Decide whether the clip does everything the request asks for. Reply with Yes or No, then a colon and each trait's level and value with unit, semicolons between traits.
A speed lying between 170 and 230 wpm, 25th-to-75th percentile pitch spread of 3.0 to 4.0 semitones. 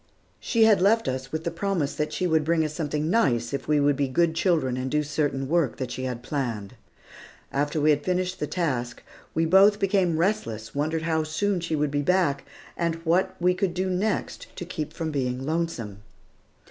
No: average, 200 wpm; average, 4.5 semitones